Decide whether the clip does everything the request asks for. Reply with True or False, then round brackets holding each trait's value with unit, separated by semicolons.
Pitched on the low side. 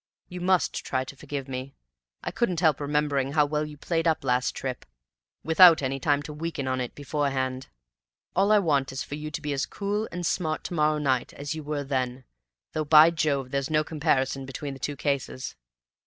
False (145 Hz)